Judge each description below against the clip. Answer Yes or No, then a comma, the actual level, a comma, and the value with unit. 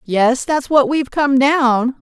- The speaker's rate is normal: Yes, average, 175 wpm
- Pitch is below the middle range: No, very high, 265 Hz